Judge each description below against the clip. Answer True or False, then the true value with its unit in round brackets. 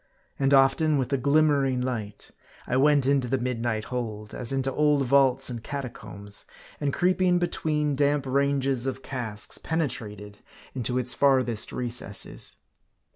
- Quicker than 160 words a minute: False (135 wpm)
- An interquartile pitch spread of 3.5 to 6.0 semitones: False (2.8 semitones)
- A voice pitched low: True (130 Hz)